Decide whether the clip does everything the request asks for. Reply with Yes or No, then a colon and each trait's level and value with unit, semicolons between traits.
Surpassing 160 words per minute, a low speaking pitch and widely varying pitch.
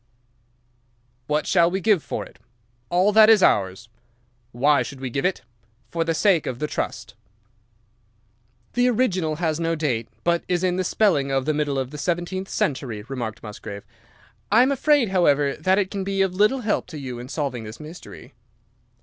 No: average, 180 wpm; medium, 165 Hz; wide, 6.0 semitones